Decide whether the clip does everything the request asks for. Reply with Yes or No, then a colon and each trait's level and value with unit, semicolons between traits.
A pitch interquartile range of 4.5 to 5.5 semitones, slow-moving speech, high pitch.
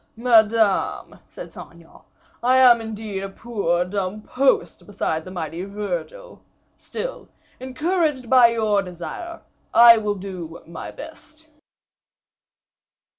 Yes: average, 5.1 semitones; slow, 115 wpm; high, 220 Hz